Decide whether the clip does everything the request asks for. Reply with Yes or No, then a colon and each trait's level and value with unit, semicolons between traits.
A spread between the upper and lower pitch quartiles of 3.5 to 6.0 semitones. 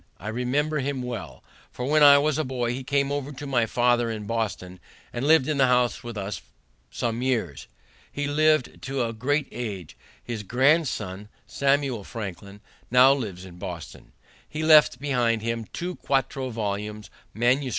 Yes: average, 4.2 semitones